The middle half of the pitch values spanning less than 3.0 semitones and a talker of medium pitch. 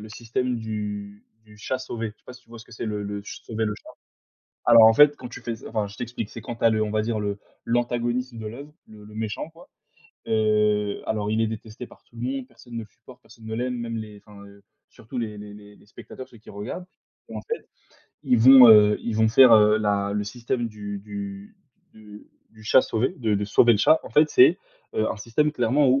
No: narrow, 2.4 semitones; low, 110 Hz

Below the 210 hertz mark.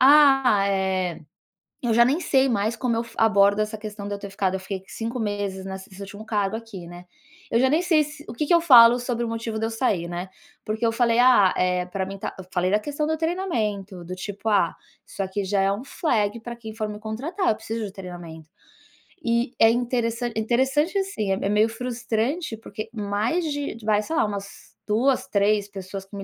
No: high, 220 Hz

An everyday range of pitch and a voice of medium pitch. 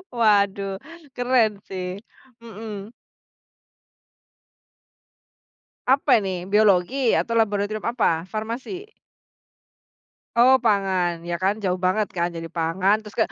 No: average, 3.7 semitones; high, 205 Hz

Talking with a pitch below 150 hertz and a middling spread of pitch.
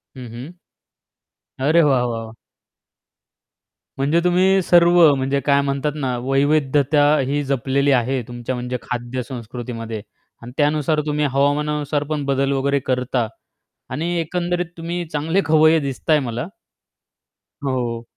Yes: medium, 140 Hz; average, 3.3 semitones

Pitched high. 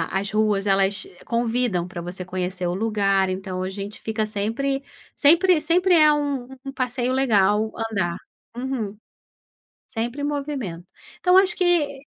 Yes: high, 225 Hz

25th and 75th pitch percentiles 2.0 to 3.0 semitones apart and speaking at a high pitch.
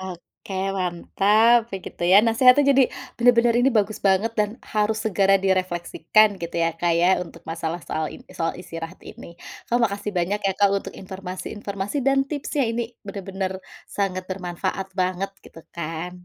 No: average, 3.4 semitones; high, 195 Hz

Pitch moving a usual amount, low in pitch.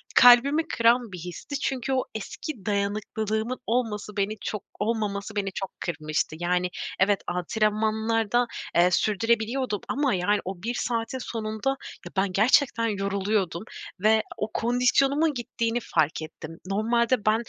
No: average, 3.2 semitones; high, 215 Hz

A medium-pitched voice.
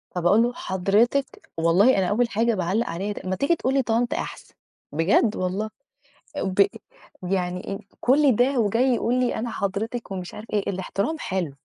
No: high, 210 Hz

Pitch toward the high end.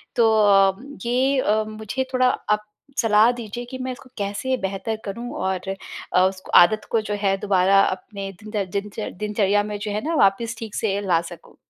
Yes: high, 210 Hz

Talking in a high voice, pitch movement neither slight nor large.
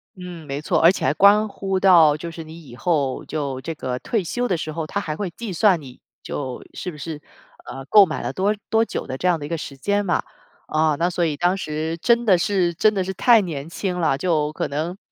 No: medium, 170 Hz; average, 4.1 semitones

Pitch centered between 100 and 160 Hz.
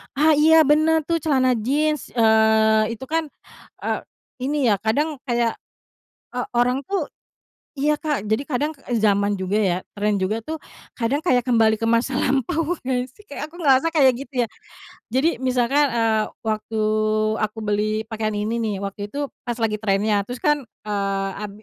No: high, 240 Hz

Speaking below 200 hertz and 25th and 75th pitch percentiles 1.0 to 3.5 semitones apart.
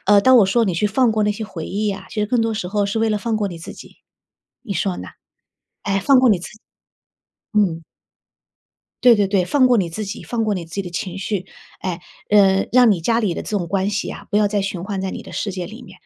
No: high, 205 Hz; narrow, 2.6 semitones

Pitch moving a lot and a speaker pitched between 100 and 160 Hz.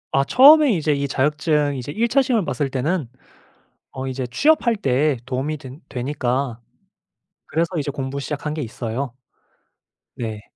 No: average, 3.5 semitones; medium, 140 Hz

